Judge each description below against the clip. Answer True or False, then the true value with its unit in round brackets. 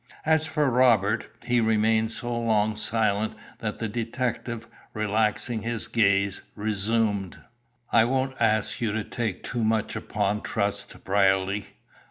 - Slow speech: True (130 wpm)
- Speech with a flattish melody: True (2.2 semitones)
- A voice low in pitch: True (110 Hz)